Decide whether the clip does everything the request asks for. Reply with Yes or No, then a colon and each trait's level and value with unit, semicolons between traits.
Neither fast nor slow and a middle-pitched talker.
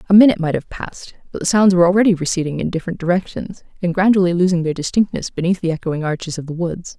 No: fast, 225 wpm; medium, 175 Hz